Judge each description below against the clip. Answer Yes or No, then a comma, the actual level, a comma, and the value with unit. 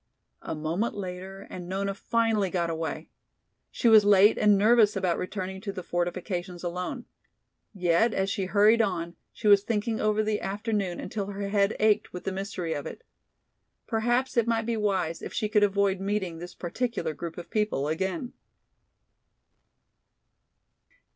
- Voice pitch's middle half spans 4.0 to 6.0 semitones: No, average, 3.0 semitones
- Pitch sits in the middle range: No, high, 195 Hz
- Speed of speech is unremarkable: Yes, average, 155 wpm